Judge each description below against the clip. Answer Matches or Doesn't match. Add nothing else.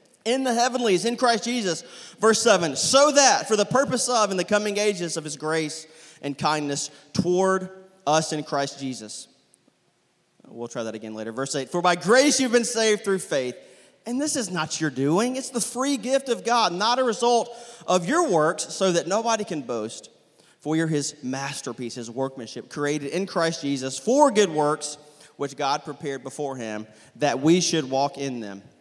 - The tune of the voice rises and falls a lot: Matches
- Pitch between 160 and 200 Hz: Matches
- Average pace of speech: Matches